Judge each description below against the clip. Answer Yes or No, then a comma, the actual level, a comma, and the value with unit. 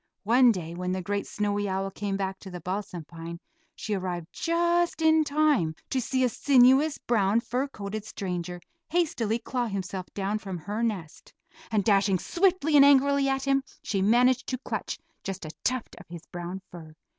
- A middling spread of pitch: No, wide, 5.9 semitones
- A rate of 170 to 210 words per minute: Yes, average, 180 wpm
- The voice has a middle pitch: No, high, 210 Hz